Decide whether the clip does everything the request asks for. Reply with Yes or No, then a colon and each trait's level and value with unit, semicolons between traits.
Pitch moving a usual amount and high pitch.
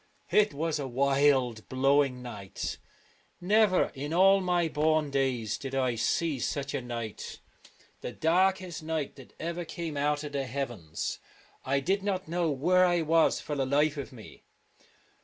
No: average, 4.2 semitones; medium, 145 Hz